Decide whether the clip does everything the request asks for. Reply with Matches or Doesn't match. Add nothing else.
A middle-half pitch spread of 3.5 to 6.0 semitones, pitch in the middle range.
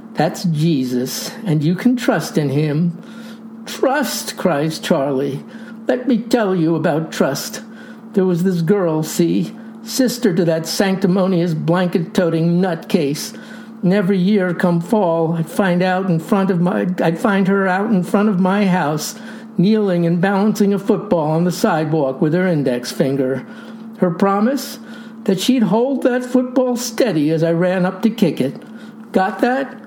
Doesn't match